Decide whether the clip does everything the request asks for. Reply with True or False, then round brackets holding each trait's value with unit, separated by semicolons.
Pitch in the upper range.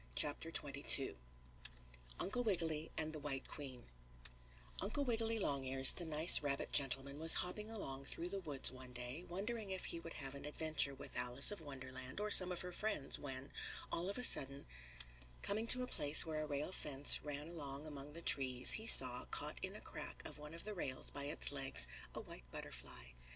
False (150 Hz)